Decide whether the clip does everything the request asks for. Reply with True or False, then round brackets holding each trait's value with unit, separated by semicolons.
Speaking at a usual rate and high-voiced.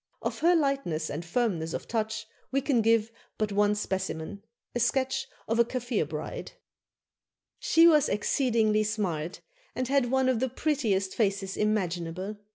True (150 wpm; 215 Hz)